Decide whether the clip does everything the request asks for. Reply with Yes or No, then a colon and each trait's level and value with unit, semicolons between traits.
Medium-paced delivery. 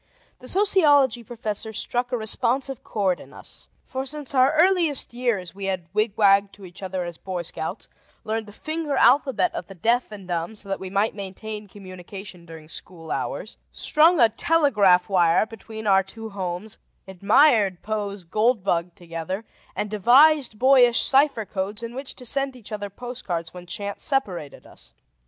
Yes: average, 165 wpm